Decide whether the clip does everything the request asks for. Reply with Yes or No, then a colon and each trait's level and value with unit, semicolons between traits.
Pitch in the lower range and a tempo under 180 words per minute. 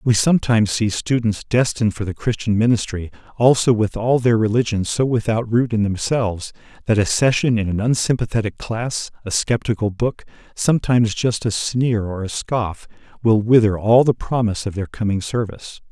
Yes: low, 110 Hz; average, 170 wpm